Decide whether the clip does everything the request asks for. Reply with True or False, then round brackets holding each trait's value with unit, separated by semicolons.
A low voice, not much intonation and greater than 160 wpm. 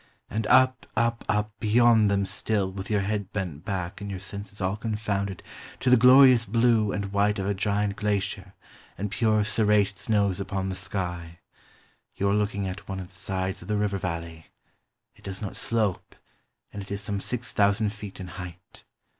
True (100 Hz; 1.9 semitones; 185 wpm)